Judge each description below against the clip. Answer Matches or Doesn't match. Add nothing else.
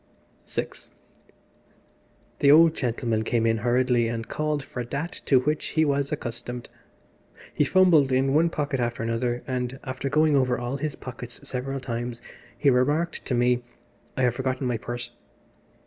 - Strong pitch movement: Doesn't match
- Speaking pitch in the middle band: Doesn't match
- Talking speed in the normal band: Matches